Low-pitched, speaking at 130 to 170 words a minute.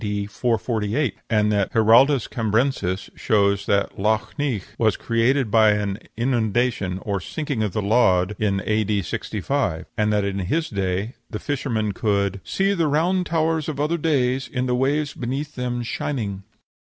Yes: low, 115 Hz; average, 150 wpm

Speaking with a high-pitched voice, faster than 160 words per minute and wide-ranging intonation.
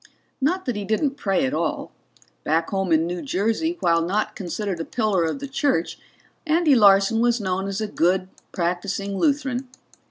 Yes: high, 200 Hz; average, 170 wpm; wide, 6.0 semitones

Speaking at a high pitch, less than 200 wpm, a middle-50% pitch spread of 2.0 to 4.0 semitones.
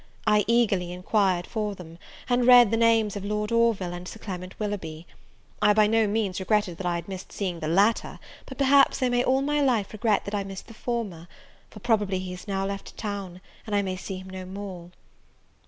No: high, 205 Hz; fast, 205 wpm; average, 3.3 semitones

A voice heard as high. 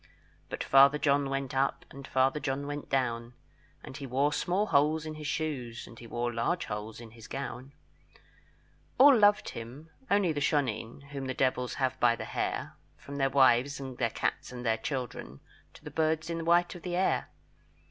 No: low, 135 Hz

